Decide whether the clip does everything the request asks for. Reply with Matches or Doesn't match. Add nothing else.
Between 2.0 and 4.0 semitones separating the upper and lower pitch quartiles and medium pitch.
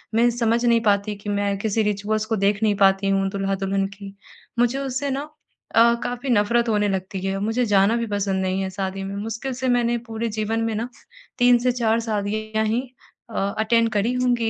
Doesn't match